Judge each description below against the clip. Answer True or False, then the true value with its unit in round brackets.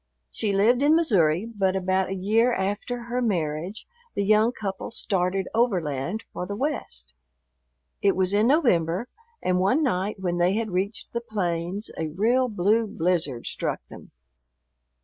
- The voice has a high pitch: True (195 Hz)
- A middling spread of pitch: True (4.1 semitones)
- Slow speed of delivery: False (150 wpm)